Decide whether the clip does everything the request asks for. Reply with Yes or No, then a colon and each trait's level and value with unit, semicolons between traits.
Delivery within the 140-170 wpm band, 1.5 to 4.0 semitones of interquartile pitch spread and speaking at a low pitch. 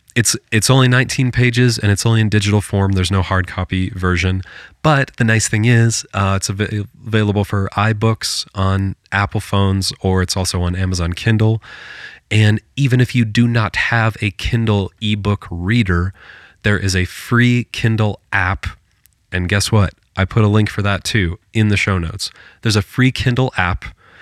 No: average, 180 wpm; average, 3.0 semitones; low, 105 Hz